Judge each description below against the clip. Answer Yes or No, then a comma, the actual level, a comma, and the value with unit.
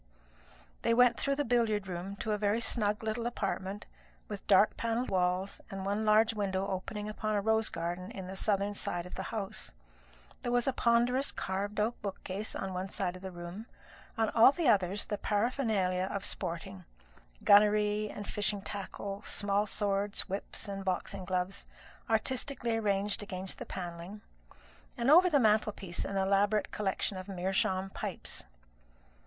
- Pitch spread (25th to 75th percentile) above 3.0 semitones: No, narrow, 2.4 semitones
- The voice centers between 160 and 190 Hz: No, high, 205 Hz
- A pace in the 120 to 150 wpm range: No, average, 160 wpm